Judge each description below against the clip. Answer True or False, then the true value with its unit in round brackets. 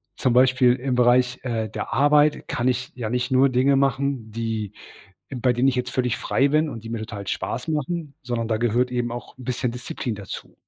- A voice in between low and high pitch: False (125 Hz)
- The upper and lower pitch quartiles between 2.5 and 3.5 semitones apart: False (2.1 semitones)